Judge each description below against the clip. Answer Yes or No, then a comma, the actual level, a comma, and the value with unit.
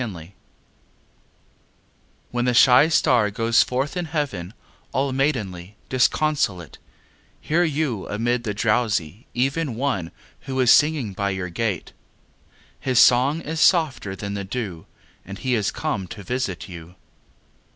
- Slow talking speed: Yes, slow, 130 wpm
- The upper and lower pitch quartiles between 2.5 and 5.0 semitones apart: No, wide, 5.4 semitones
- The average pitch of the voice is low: Yes, low, 120 Hz